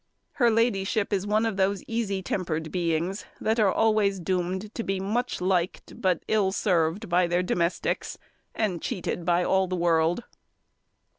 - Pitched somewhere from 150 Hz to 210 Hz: Yes, high, 190 Hz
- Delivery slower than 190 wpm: Yes, average, 155 wpm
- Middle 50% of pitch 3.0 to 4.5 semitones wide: Yes, average, 3.4 semitones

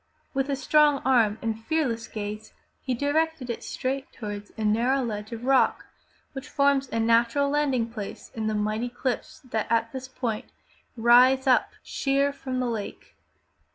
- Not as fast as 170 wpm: Yes, average, 160 wpm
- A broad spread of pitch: No, average, 3.4 semitones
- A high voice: Yes, high, 245 Hz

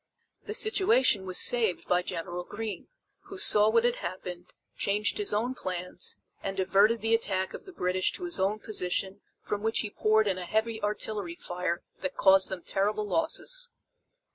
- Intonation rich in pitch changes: No, average, 3.6 semitones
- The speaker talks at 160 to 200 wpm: Yes, average, 170 wpm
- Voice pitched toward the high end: Yes, high, 205 Hz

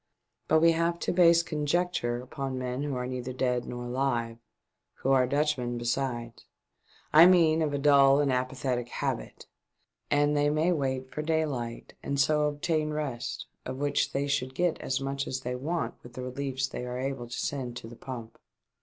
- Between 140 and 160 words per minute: No, average, 180 wpm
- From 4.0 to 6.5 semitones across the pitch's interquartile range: No, average, 3.0 semitones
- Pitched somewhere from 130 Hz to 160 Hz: Yes, low, 135 Hz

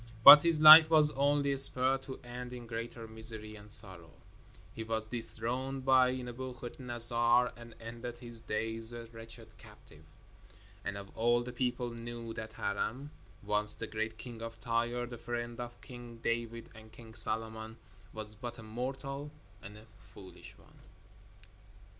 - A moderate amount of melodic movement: No, narrow, 1.9 semitones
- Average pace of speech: Yes, average, 145 wpm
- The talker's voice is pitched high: No, low, 120 Hz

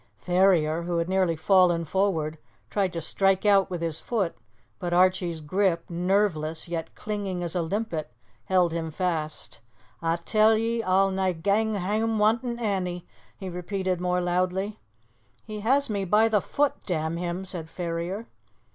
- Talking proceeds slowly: No, average, 155 wpm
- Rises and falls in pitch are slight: No, average, 3.2 semitones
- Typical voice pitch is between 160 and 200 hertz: Yes, medium, 185 Hz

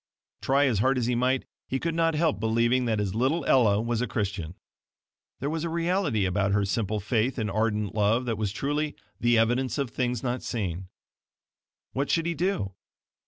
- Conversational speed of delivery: Yes, average, 190 wpm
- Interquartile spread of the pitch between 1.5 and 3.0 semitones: No, average, 4.6 semitones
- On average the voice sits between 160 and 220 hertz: No, low, 120 Hz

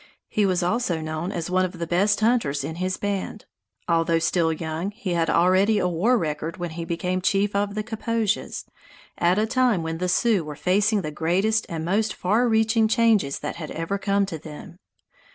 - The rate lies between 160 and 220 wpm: Yes, average, 195 wpm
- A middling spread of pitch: Yes, average, 4.2 semitones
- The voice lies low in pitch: No, medium, 185 Hz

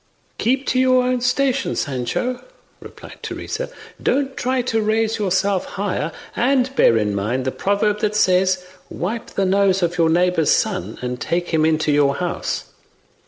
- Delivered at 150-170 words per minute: Yes, average, 160 wpm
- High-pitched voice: Yes, high, 195 Hz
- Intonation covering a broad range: Yes, wide, 6.9 semitones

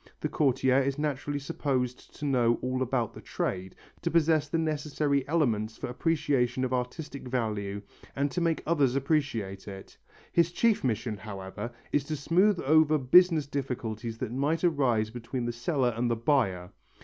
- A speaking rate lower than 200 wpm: Yes, average, 160 wpm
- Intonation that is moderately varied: Yes, average, 4.4 semitones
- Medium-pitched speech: No, low, 130 Hz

